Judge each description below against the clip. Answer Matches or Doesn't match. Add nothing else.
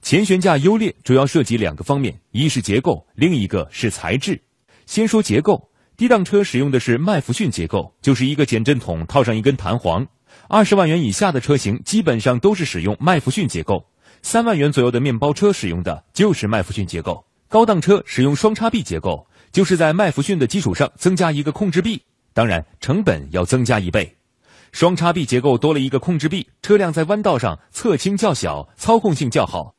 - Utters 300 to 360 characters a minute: Matches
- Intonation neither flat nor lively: Doesn't match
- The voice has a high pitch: Doesn't match